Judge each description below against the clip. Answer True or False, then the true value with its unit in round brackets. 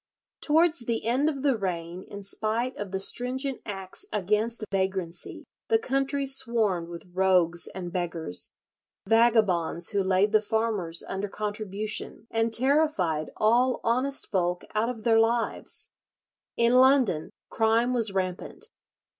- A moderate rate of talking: False (130 wpm)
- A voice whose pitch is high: True (215 Hz)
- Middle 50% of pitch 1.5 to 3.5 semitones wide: False (4.5 semitones)